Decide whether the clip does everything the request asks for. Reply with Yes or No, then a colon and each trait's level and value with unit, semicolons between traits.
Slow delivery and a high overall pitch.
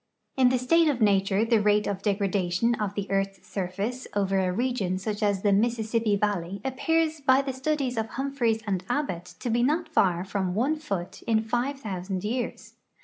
No: average, 185 wpm; high, 220 Hz